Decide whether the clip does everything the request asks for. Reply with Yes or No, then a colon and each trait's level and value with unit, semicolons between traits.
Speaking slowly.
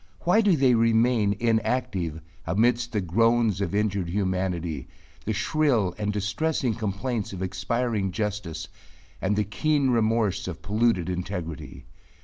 Yes: slow, 125 wpm